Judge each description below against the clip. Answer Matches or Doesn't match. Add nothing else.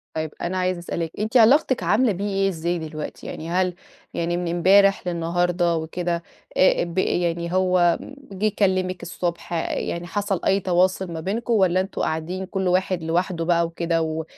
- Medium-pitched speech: Matches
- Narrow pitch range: Matches